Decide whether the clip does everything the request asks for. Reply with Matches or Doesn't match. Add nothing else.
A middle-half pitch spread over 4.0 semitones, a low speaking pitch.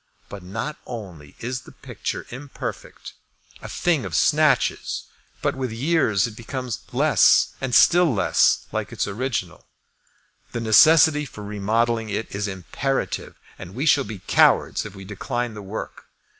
Matches